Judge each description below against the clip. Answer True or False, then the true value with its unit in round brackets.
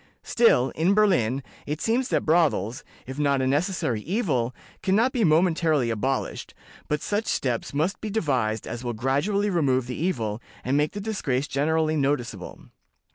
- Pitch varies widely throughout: True (6.7 semitones)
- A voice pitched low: False (150 Hz)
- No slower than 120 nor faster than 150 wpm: False (160 wpm)